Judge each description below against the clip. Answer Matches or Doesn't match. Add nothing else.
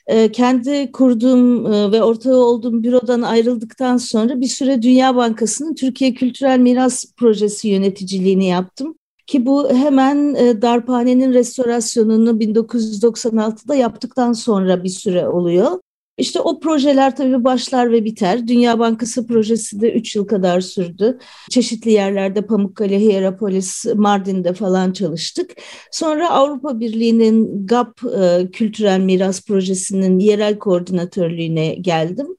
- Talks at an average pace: Matches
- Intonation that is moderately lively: Matches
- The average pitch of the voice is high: Matches